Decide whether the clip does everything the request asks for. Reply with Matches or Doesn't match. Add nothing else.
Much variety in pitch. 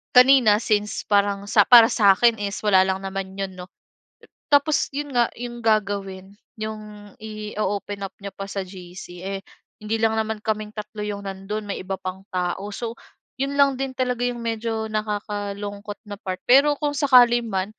Doesn't match